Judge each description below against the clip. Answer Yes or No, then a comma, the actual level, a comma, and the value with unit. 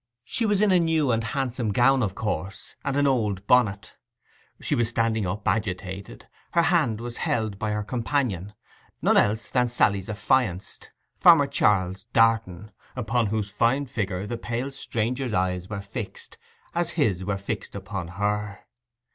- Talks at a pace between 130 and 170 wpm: Yes, average, 155 wpm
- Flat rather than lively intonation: No, average, 4.2 semitones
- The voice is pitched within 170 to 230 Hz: No, low, 110 Hz